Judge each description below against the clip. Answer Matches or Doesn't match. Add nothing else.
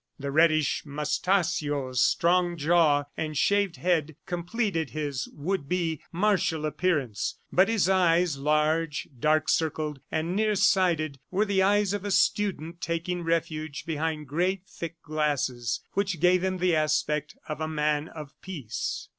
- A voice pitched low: Doesn't match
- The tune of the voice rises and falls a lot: Doesn't match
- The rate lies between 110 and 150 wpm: Matches